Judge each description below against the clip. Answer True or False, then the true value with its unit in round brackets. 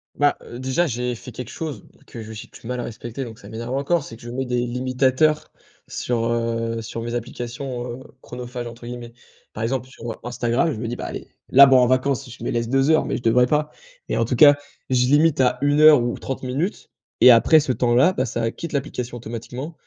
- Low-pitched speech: True (125 Hz)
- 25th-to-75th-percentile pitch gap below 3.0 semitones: True (2.4 semitones)